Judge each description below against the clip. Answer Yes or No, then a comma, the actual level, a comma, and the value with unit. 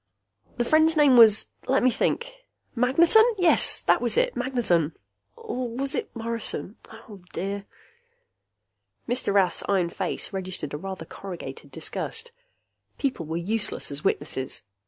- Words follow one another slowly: Yes, slow, 130 wpm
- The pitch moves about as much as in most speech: No, wide, 6.2 semitones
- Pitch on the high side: Yes, high, 225 Hz